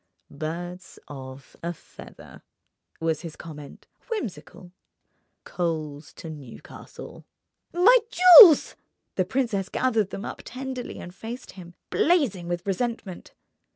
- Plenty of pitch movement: Yes, wide, 7.5 semitones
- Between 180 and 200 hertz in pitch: Yes, medium, 185 Hz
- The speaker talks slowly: Yes, slow, 110 wpm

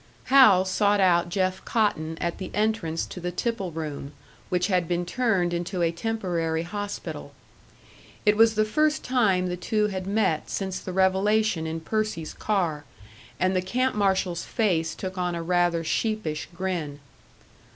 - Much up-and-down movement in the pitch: No, average, 3.6 semitones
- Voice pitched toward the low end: No, medium, 185 Hz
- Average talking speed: Yes, average, 155 wpm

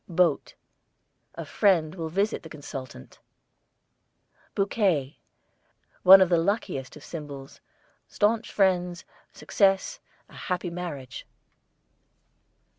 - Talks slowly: Yes, slow, 95 wpm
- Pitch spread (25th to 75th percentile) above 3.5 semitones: Yes, average, 4.3 semitones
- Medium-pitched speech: Yes, medium, 175 Hz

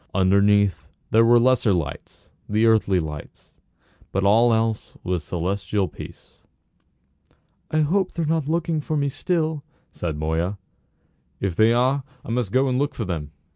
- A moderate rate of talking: Yes, average, 155 wpm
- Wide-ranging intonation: Yes, wide, 6.5 semitones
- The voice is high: No, low, 110 Hz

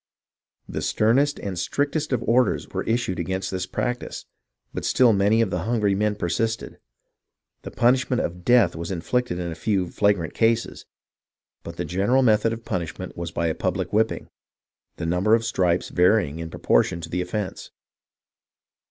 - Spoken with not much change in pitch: No, average, 4.6 semitones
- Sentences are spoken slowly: No, average, 160 wpm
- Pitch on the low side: Yes, low, 100 Hz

